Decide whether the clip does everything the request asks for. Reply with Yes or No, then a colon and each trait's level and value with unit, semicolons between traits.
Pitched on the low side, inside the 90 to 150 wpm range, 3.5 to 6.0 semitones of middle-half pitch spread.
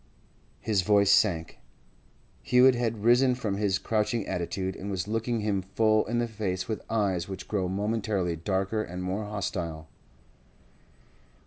No: low, 100 Hz; average, 140 wpm; average, 3.0 semitones